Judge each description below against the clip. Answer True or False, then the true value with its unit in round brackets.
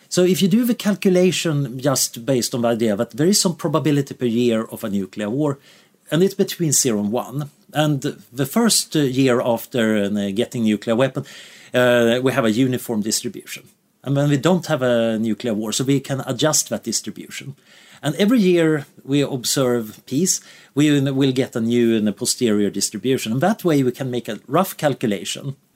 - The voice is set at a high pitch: False (135 Hz)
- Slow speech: False (185 wpm)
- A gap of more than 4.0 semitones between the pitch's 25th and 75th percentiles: True (4.7 semitones)